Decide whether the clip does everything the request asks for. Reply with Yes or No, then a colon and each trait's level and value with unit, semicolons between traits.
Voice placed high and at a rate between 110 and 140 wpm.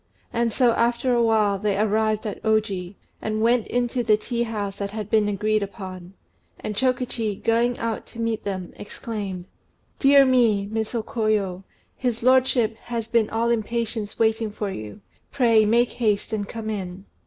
No: high, 220 Hz; average, 165 wpm